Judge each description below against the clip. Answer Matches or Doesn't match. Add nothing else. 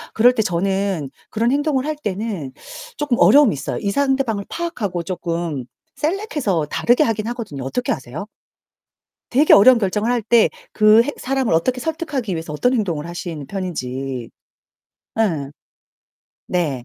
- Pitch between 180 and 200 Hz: Doesn't match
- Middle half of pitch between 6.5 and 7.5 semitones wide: Matches